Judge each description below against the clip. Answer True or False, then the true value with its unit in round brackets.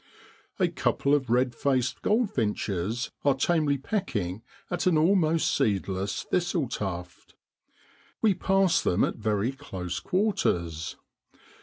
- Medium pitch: False (130 Hz)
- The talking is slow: True (115 wpm)